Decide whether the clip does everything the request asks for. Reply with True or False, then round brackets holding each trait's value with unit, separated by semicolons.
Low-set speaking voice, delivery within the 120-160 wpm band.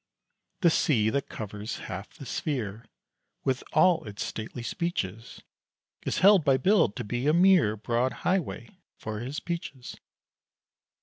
True (130 Hz; 135 wpm)